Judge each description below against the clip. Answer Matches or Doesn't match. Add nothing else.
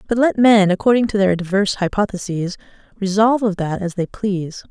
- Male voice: Doesn't match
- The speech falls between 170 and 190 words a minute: Matches